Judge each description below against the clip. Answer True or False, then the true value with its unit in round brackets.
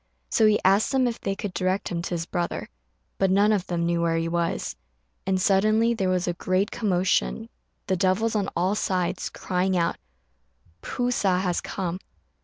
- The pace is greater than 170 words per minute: True (185 wpm)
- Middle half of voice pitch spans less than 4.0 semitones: True (2.7 semitones)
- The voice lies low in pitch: False (185 Hz)